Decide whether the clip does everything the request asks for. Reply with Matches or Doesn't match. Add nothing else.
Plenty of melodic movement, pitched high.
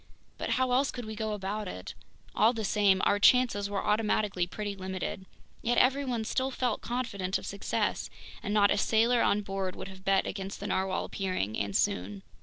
Doesn't match